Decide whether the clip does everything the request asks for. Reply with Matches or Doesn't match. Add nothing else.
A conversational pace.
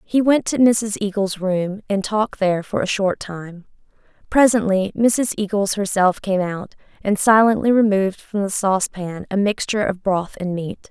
Matches